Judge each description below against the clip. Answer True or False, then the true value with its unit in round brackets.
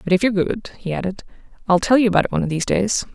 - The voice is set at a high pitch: True (195 Hz)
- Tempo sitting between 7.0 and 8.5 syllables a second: True (7.8 syllables/s)